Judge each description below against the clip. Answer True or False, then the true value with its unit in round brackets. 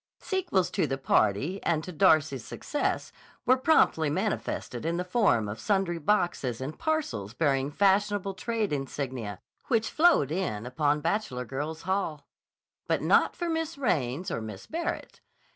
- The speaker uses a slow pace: False (145 wpm)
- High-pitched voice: False (165 Hz)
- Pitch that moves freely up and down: True (7.5 semitones)